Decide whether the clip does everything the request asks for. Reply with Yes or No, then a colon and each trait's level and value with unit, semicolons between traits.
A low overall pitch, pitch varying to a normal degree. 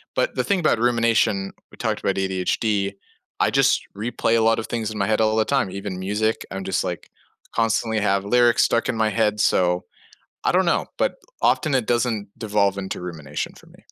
Yes: low, 110 Hz; average, 3.0 semitones